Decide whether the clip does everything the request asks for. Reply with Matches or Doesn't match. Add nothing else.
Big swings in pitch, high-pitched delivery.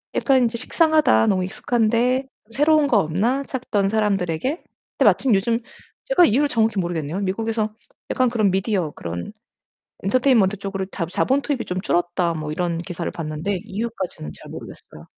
Matches